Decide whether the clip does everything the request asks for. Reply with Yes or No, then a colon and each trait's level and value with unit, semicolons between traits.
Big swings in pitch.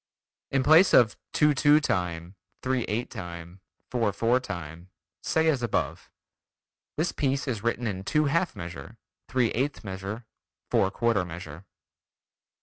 Yes: wide, 6.5 semitones